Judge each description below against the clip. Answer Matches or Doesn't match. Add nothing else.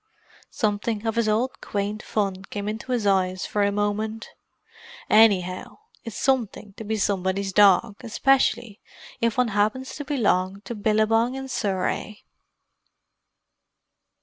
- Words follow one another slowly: Matches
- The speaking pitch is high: Matches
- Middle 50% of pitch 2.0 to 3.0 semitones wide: Matches